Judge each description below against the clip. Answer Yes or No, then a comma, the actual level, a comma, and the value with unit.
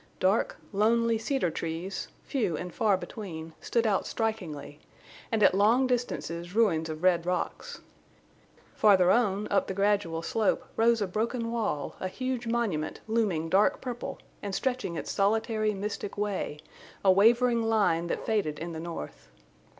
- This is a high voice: Yes, high, 205 Hz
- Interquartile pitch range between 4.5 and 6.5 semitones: Yes, average, 4.8 semitones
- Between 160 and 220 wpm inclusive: No, average, 150 wpm